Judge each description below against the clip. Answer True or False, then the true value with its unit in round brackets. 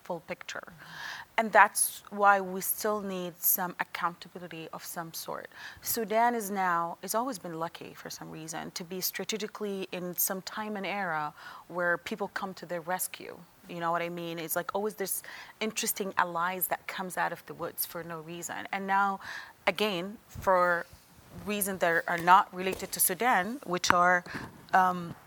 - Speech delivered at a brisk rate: False (170 wpm)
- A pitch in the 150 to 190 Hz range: True (185 Hz)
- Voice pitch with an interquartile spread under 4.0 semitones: True (2.7 semitones)